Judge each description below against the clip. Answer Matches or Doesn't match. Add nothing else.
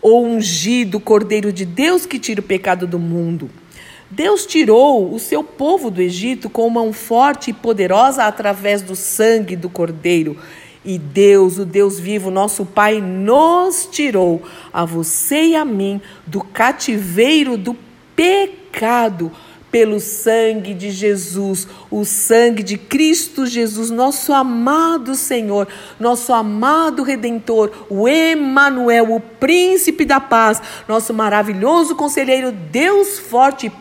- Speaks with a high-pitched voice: Matches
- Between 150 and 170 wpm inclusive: Doesn't match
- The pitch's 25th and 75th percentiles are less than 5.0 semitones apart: Doesn't match